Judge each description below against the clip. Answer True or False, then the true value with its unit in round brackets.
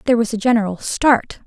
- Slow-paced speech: False (205 wpm)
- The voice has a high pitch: True (230 Hz)